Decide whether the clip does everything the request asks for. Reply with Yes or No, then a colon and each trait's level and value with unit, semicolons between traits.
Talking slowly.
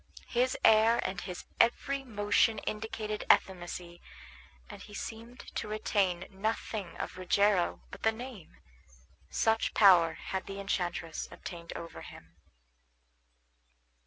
Yes: slow, 115 wpm